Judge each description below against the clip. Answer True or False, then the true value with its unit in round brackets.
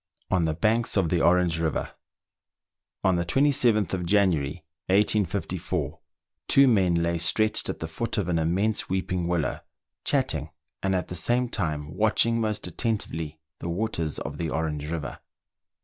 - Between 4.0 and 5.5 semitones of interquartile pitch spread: True (4.8 semitones)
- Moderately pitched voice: False (90 Hz)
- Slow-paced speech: False (150 wpm)